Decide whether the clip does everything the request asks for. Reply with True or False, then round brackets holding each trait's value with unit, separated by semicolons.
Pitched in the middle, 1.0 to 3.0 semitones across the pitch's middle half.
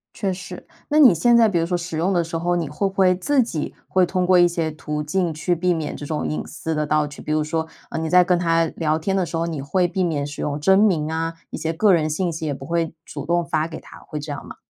True (165 Hz; 2.7 semitones)